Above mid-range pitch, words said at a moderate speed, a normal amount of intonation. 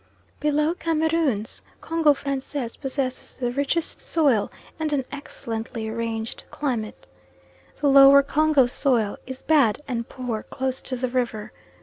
No: very high, 265 Hz; slow, 125 wpm; average, 4.0 semitones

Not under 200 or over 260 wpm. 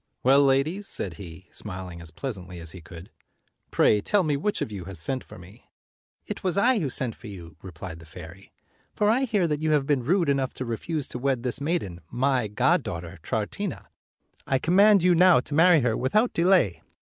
Yes: fast, 205 wpm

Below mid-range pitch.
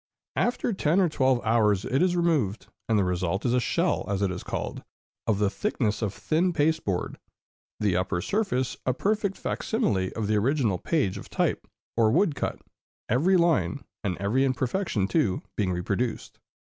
Yes: low, 120 Hz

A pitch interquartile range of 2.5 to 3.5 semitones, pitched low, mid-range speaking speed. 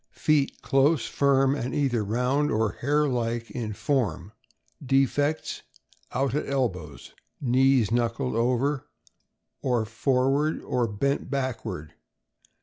No: average, 3.2 semitones; low, 130 Hz; slow, 115 wpm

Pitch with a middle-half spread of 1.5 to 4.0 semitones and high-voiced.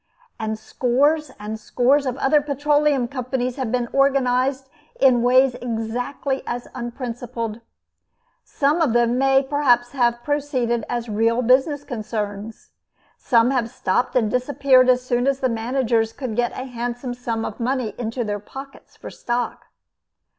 Yes: narrow, 2.5 semitones; high, 245 Hz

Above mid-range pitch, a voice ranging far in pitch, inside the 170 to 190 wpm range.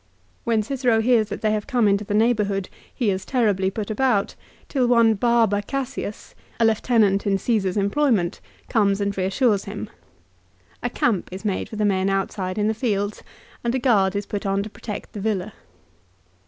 No: high, 210 Hz; average, 2.9 semitones; average, 180 wpm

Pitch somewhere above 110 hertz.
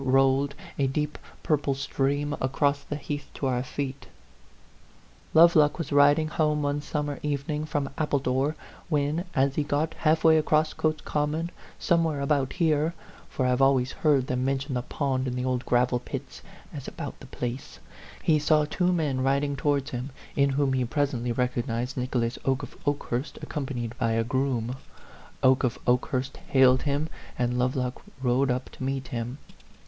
Yes: medium, 140 Hz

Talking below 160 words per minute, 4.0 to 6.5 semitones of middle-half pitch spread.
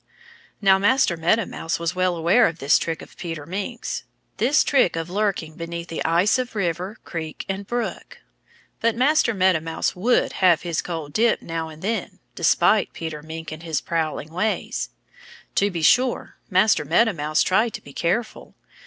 No: average, 170 wpm; average, 4.7 semitones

